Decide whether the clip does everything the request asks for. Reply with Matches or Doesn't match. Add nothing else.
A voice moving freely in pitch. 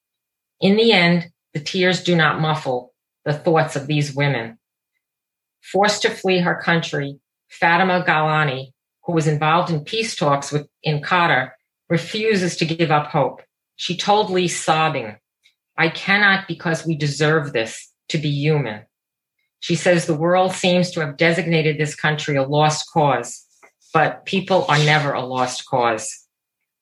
Doesn't match